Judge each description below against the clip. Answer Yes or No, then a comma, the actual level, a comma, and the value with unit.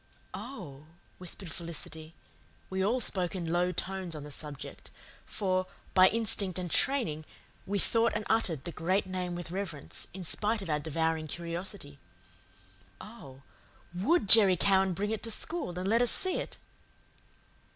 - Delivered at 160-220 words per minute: No, average, 150 wpm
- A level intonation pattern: No, average, 3.9 semitones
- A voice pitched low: No, medium, 185 Hz